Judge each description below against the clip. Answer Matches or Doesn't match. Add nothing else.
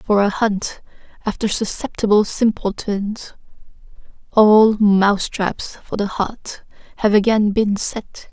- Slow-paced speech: Matches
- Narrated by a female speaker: Matches